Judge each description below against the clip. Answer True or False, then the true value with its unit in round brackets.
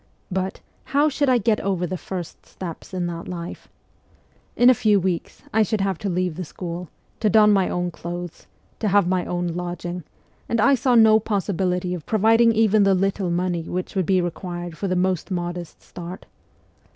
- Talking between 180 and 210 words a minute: True (190 wpm)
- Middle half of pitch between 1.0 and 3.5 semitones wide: True (3.1 semitones)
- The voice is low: False (185 Hz)